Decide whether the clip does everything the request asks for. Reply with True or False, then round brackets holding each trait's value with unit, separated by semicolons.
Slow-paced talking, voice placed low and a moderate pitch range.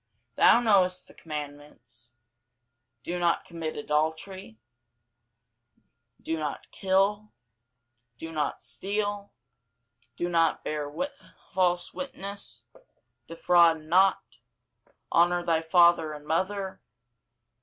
False (90 wpm; 170 Hz; 3.7 semitones)